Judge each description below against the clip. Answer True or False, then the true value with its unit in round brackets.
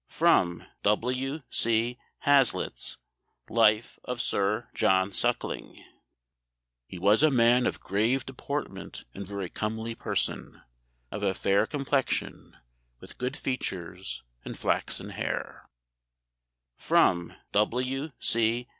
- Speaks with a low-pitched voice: True (115 Hz)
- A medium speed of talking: False (105 wpm)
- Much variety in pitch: False (4.3 semitones)